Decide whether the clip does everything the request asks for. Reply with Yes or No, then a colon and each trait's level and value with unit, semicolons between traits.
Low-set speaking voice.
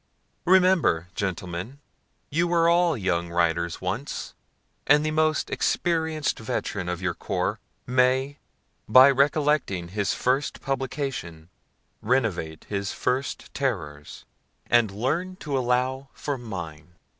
Yes: low, 125 Hz